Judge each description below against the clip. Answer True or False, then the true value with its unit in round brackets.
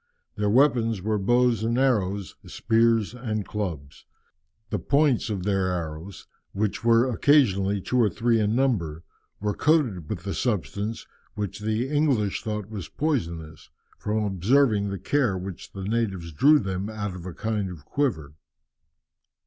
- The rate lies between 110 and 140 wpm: False (150 wpm)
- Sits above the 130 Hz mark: False (105 Hz)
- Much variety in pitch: False (4.0 semitones)